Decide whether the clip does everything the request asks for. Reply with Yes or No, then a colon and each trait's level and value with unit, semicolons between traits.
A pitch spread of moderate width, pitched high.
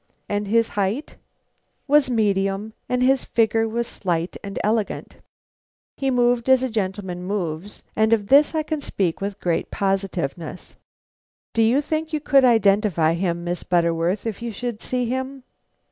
Yes: average, 4.7 semitones; high, 215 Hz